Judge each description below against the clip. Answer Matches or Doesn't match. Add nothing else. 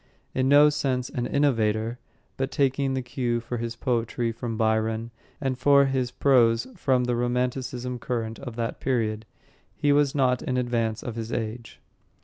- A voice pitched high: Doesn't match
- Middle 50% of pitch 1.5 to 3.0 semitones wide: Matches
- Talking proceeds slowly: Doesn't match